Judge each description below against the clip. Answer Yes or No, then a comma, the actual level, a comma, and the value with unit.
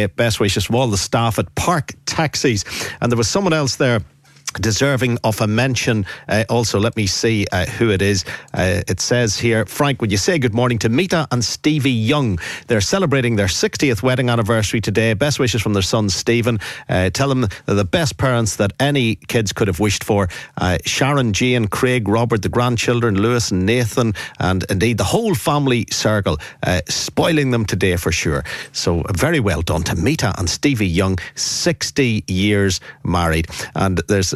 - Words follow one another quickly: No, average, 185 wpm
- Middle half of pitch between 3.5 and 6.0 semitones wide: Yes, average, 3.8 semitones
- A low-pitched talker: Yes, low, 115 Hz